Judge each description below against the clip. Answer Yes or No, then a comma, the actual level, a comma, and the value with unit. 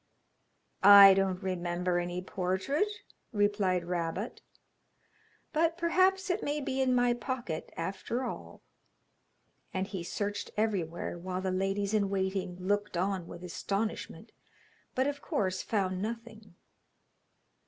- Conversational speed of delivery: No, slow, 120 wpm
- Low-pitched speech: No, high, 195 Hz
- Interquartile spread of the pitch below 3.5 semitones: No, average, 4.3 semitones